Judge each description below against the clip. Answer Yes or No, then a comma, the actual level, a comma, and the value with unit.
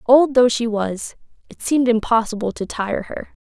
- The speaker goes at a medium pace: Yes, average, 175 wpm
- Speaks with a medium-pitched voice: No, high, 230 Hz